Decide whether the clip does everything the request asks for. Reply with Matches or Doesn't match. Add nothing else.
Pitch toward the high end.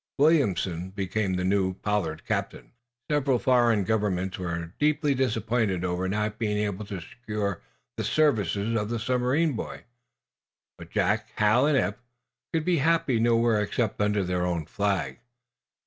Doesn't match